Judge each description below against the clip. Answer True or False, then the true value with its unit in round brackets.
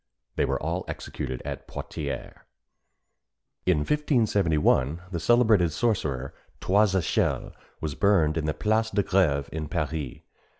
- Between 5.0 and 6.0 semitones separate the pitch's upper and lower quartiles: True (5.4 semitones)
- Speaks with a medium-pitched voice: False (85 Hz)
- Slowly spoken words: True (125 wpm)